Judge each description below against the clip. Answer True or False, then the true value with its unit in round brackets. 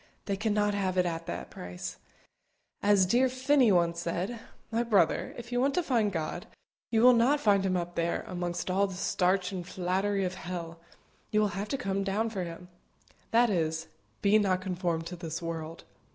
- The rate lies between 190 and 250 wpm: True (195 wpm)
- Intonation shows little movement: False (3.7 semitones)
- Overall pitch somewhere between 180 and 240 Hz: True (190 Hz)